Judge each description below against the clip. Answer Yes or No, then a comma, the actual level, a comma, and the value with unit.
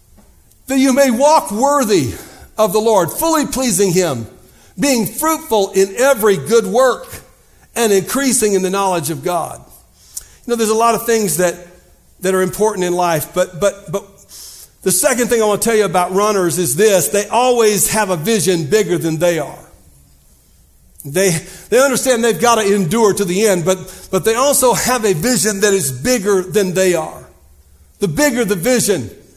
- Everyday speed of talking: Yes, average, 180 wpm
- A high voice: Yes, high, 205 Hz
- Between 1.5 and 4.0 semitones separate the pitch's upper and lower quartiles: No, average, 4.4 semitones